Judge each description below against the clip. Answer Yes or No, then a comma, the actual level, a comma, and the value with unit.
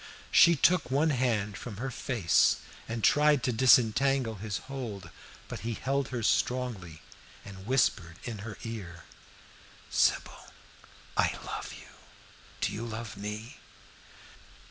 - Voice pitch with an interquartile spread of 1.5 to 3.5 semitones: No, average, 4.1 semitones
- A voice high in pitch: No, low, 115 Hz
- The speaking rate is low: Yes, slow, 125 wpm